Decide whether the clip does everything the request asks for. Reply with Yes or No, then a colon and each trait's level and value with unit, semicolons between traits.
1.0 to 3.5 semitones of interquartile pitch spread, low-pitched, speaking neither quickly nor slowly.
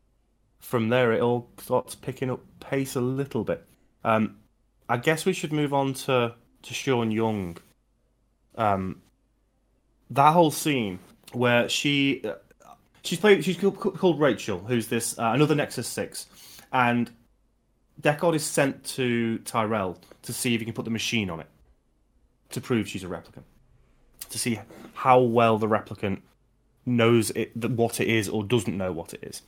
Yes: average, 2.8 semitones; low, 120 Hz; average, 155 wpm